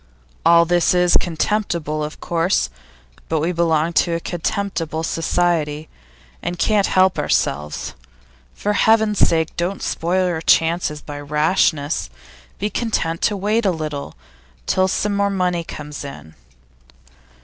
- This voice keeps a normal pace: No, slow, 130 wpm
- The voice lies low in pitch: No, medium, 170 Hz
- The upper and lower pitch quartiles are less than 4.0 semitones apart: Yes, average, 3.4 semitones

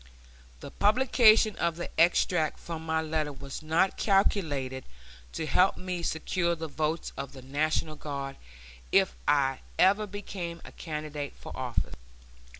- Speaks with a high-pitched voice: No, medium, 160 Hz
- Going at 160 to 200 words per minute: No, average, 140 wpm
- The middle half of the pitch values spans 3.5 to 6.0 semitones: Yes, average, 3.9 semitones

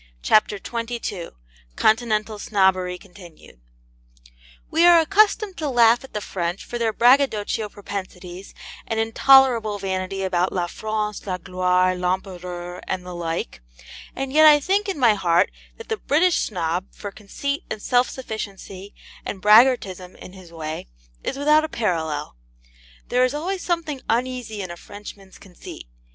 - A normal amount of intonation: No, wide, 5.7 semitones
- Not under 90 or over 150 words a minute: Yes, average, 145 wpm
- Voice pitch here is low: No, high, 210 Hz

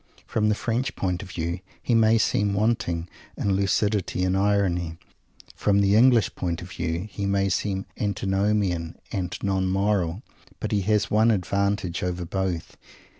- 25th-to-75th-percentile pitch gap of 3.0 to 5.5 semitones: No, narrow, 2.5 semitones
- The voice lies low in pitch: Yes, low, 100 Hz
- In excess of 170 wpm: No, average, 155 wpm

